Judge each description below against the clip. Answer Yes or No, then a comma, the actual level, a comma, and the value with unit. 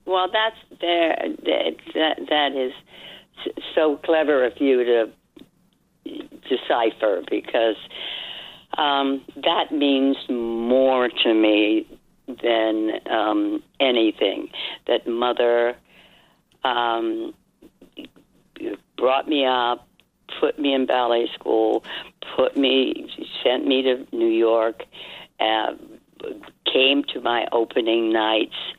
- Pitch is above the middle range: No, low, 130 Hz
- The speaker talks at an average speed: No, slow, 100 wpm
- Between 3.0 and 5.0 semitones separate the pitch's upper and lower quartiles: No, wide, 5.6 semitones